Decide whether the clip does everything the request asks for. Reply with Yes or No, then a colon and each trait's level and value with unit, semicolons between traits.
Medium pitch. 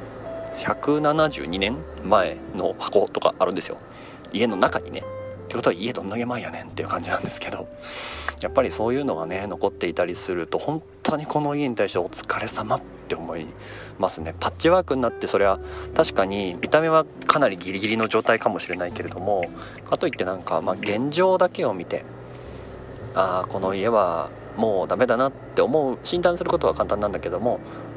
No: low, 110 Hz